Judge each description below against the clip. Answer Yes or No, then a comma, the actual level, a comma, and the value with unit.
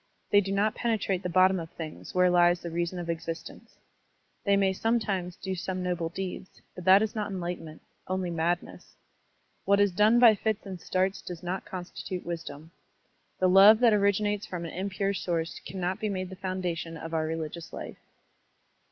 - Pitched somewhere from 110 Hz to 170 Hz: No, medium, 185 Hz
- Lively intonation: No, narrow, 2.4 semitones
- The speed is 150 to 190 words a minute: Yes, average, 180 wpm